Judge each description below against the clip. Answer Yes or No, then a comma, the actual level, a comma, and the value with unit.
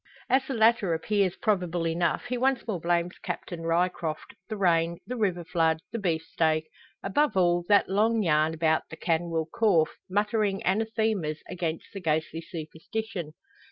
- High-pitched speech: No, medium, 175 Hz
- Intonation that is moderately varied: Yes, average, 4.6 semitones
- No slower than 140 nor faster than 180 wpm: Yes, average, 150 wpm